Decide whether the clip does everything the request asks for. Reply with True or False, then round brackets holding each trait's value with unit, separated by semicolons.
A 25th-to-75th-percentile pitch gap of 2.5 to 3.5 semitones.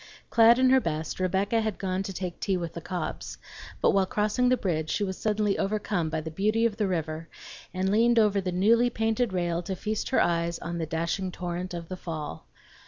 False (3.9 semitones)